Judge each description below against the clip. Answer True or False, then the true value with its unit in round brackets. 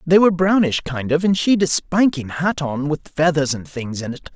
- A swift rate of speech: True (235 wpm)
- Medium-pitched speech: True (155 Hz)